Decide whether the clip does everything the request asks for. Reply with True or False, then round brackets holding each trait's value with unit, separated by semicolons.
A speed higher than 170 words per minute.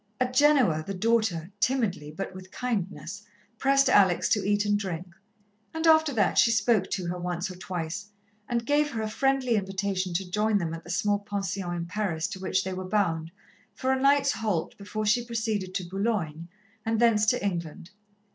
True (185 wpm)